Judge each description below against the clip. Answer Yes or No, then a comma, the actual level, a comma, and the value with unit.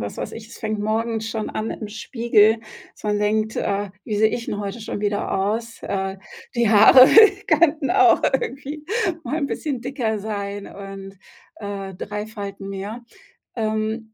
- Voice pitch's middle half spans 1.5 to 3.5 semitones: Yes, narrow, 2.5 semitones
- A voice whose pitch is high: Yes, high, 215 Hz